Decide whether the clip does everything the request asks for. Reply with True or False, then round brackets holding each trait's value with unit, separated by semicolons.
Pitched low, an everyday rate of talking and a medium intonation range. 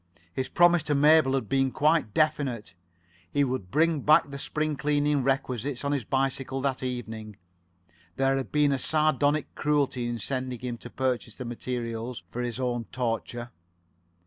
True (130 Hz; 160 wpm; 3.1 semitones)